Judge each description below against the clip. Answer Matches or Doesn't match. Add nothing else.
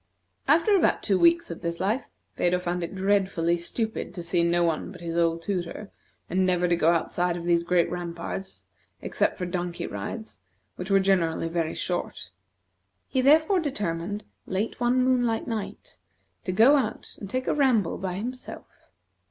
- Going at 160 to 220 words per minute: Matches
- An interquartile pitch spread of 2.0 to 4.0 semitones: Doesn't match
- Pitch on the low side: Doesn't match